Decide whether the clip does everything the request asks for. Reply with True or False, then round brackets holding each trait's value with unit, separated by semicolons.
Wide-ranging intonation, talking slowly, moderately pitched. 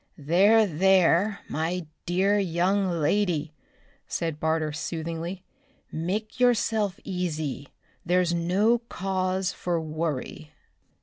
False (3.2 semitones; 95 wpm; 180 Hz)